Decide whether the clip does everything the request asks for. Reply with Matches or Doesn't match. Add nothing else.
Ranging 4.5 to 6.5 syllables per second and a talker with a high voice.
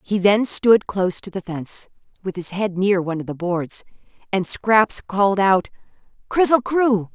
Matches